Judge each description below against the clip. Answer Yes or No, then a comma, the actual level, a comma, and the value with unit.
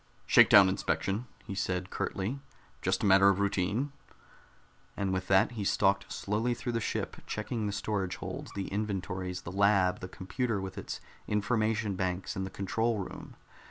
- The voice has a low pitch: Yes, low, 100 Hz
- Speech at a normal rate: Yes, average, 160 wpm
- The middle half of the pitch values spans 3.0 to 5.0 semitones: No, narrow, 2.5 semitones